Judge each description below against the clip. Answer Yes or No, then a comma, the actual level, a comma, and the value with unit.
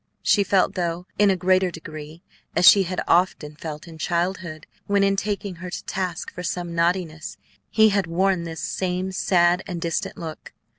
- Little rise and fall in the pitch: Yes, narrow, 2.2 semitones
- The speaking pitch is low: No, medium, 180 Hz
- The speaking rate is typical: Yes, average, 180 wpm